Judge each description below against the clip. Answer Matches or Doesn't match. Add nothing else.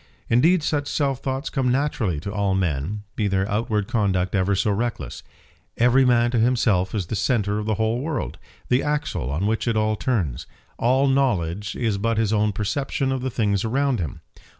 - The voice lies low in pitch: Matches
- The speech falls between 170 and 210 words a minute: Matches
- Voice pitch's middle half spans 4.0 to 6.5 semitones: Matches